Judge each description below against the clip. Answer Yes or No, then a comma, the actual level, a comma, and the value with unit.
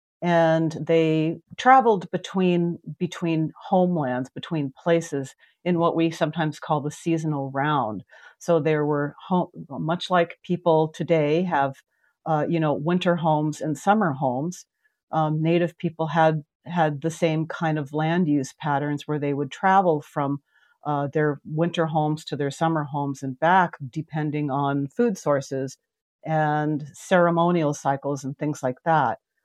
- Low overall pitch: No, medium, 155 Hz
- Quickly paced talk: No, average, 145 wpm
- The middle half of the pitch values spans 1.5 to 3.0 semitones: Yes, narrow, 2.6 semitones